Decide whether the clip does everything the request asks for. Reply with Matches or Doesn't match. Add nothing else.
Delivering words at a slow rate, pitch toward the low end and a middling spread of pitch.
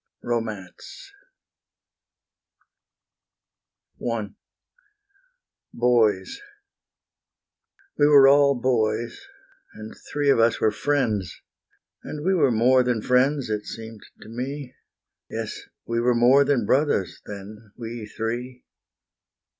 Matches